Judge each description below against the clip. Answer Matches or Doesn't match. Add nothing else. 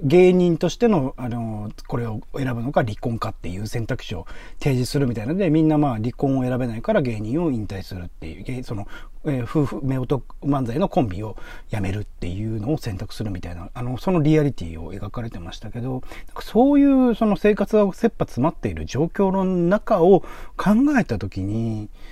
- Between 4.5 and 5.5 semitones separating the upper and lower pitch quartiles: Doesn't match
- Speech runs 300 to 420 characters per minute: Matches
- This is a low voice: Matches